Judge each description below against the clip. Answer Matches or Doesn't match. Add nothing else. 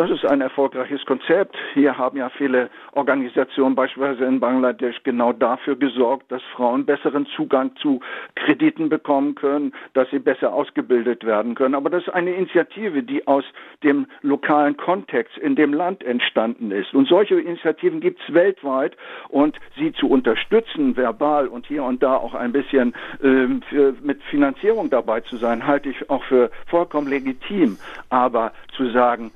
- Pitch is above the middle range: Doesn't match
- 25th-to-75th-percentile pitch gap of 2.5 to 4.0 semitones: Doesn't match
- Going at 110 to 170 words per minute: Matches